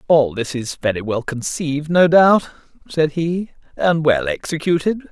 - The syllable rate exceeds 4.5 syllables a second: No, 4.4 syllables/s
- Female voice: No, male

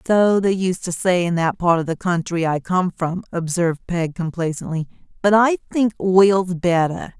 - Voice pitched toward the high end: No, medium, 180 Hz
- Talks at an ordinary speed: Yes, average, 185 wpm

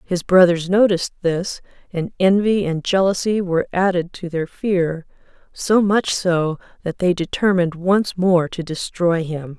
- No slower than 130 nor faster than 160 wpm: Yes, average, 150 wpm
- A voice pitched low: No, medium, 180 Hz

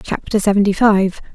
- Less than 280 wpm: Yes, slow, 135 wpm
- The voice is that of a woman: Yes, female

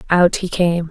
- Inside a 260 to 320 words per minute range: No, average, 200 wpm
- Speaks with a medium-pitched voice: Yes, medium, 175 Hz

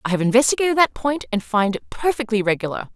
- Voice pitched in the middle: No, high, 235 Hz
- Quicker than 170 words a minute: Yes, fast, 205 wpm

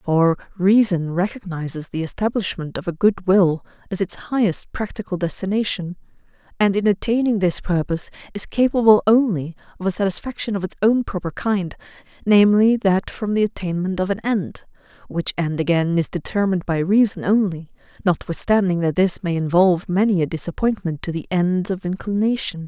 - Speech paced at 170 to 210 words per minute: No, average, 155 wpm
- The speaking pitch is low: No, high, 190 Hz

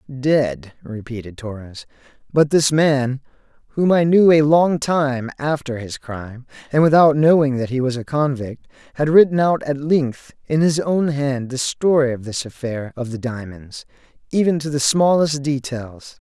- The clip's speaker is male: Yes, male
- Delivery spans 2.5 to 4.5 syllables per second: Yes, 4.4 syllables/s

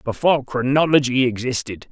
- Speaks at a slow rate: Yes, slow, 95 wpm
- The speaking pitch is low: Yes, low, 130 Hz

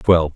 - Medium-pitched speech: No, very low, 80 Hz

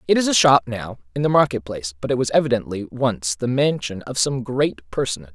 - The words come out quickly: Yes, fast, 225 wpm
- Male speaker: Yes, male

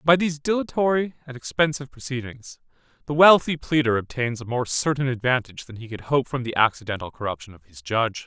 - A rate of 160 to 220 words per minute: Yes, average, 180 wpm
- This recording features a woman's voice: No, male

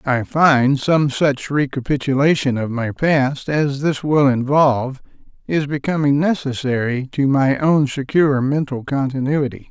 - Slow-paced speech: Yes, slow, 130 wpm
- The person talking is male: Yes, male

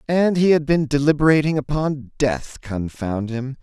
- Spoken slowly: Yes, slow, 130 wpm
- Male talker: Yes, male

